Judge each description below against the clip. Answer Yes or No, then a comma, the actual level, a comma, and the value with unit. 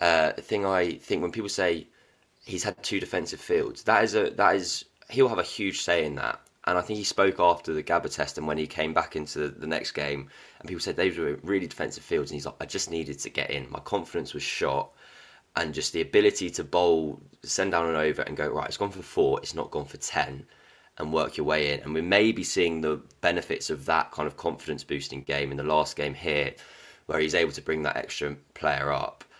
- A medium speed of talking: No, fast, 245 wpm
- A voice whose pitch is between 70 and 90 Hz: Yes, very low, 85 Hz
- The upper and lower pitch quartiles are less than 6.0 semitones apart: No, wide, 6.9 semitones